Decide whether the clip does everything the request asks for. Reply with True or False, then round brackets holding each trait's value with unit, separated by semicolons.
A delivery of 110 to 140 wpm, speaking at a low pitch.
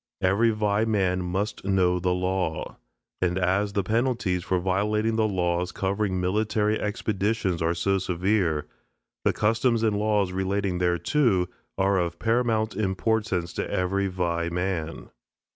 True (135 wpm; 95 Hz)